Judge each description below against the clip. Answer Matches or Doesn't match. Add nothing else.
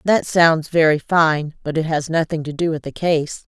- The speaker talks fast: Matches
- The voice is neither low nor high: Matches